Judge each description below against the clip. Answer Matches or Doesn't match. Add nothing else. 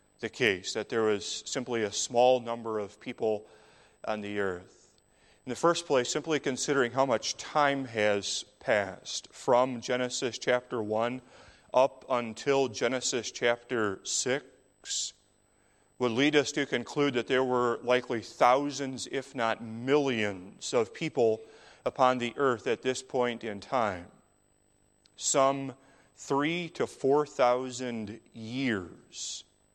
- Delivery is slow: Matches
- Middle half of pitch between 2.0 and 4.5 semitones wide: Matches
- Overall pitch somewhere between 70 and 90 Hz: Doesn't match